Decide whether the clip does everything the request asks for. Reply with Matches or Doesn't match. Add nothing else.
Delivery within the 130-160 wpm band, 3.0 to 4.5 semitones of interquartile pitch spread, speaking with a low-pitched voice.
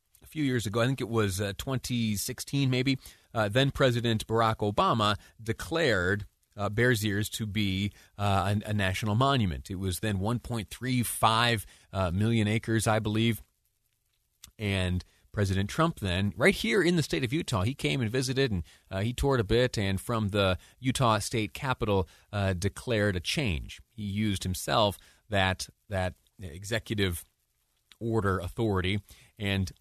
Matches